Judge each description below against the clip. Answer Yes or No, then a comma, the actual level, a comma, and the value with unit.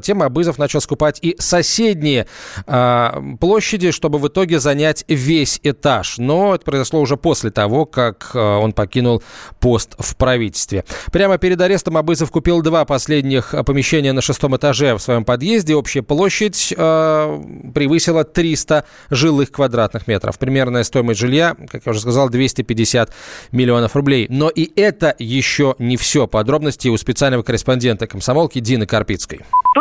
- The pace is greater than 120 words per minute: Yes, average, 145 wpm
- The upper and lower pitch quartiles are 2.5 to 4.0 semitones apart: No, average, 4.8 semitones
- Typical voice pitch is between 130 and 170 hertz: Yes, medium, 140 Hz